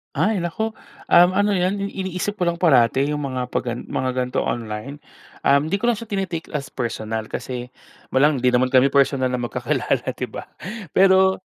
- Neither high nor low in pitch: Yes, medium, 145 Hz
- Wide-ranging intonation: Yes, wide, 6.9 semitones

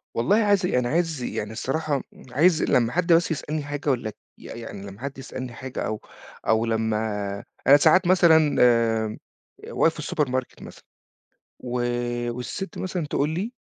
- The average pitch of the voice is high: No, medium, 140 Hz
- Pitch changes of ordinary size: No, wide, 5.7 semitones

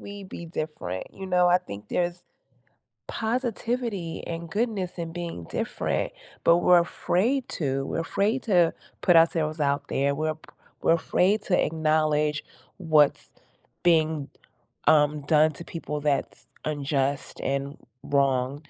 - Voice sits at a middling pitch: Yes, medium, 160 Hz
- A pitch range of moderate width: Yes, average, 3.5 semitones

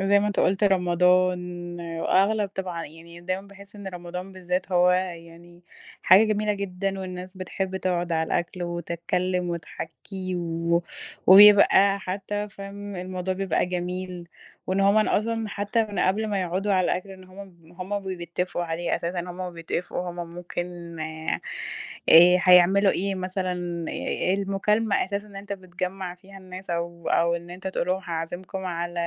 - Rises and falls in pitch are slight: Yes, narrow, 2.1 semitones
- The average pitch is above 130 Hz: Yes, medium, 185 Hz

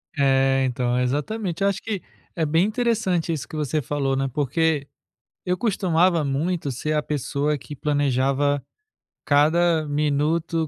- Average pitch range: Yes, average, 3.5 semitones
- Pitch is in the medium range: Yes, medium, 150 Hz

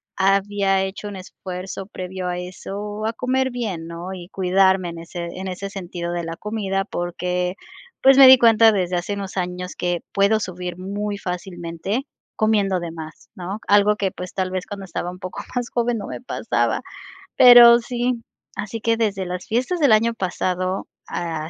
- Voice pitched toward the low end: No, high, 190 Hz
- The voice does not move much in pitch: No, average, 3.1 semitones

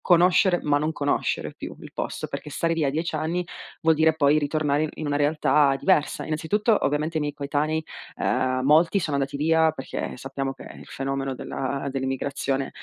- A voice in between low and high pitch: Yes, medium, 150 Hz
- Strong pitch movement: No, narrow, 2.5 semitones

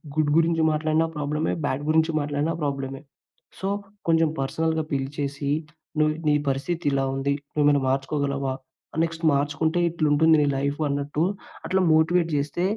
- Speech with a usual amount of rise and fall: No, narrow, 2.3 semitones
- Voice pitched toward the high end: No, medium, 150 Hz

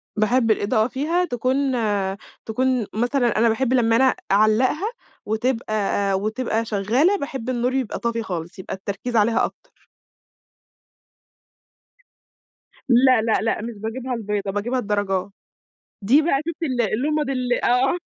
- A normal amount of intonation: Yes, average, 3.3 semitones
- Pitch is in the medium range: No, high, 235 Hz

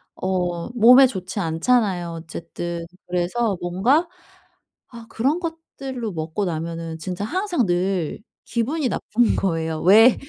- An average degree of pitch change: No, wide, 6.0 semitones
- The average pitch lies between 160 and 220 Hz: Yes, high, 190 Hz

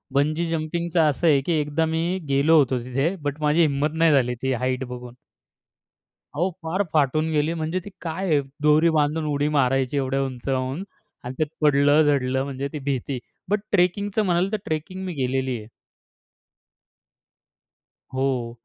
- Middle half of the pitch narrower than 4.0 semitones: Yes, average, 3.5 semitones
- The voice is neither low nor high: Yes, medium, 150 Hz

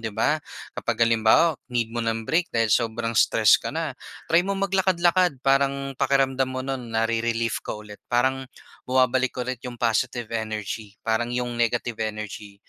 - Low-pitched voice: Yes, low, 120 Hz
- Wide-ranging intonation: No, average, 3.0 semitones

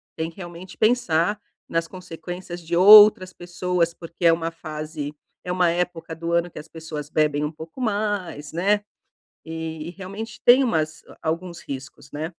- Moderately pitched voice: Yes, medium, 170 Hz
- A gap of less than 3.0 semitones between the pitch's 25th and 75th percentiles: Yes, narrow, 2.5 semitones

